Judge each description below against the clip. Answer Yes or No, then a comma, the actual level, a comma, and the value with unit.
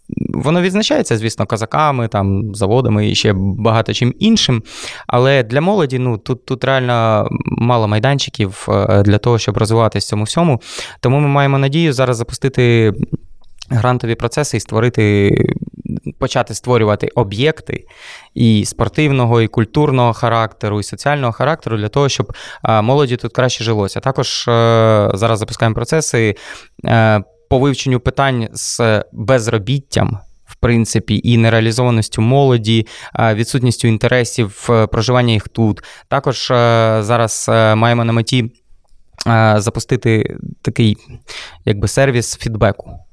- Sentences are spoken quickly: No, average, 115 wpm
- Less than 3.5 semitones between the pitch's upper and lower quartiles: Yes, average, 2.9 semitones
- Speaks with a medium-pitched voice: No, low, 115 Hz